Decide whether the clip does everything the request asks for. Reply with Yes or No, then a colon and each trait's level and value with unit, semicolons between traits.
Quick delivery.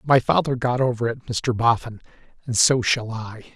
No: average, 185 wpm